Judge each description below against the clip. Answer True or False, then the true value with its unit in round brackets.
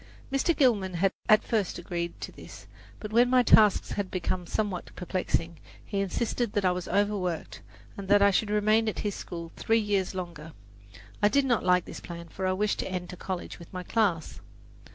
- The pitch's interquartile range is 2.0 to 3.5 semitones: True (3.1 semitones)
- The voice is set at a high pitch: True (195 Hz)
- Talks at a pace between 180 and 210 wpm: True (190 wpm)